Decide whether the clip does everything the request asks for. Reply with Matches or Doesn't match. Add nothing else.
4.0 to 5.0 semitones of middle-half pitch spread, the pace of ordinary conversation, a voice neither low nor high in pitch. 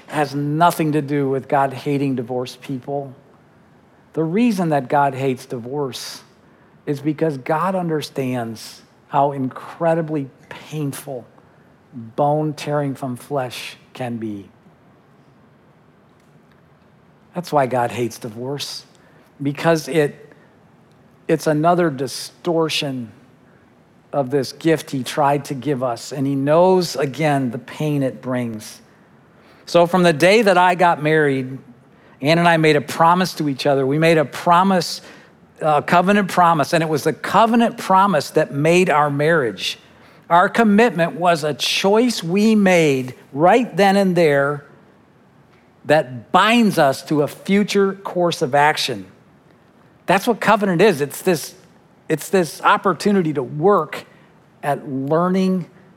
Doesn't match